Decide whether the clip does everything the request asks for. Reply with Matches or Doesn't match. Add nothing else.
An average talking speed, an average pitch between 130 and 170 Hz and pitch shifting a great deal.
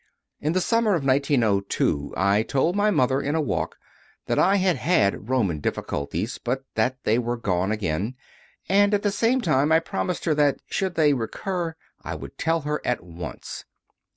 Matches